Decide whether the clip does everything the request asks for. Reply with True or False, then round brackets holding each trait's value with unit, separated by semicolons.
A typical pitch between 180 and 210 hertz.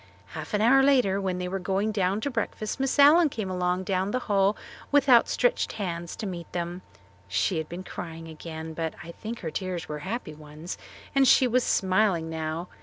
True (190 Hz)